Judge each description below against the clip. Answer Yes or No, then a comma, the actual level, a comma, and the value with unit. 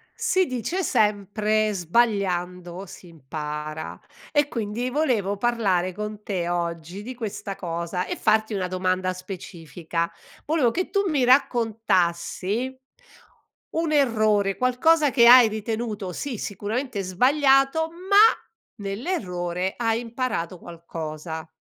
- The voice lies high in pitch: Yes, high, 210 Hz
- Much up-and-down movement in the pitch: Yes, wide, 5.9 semitones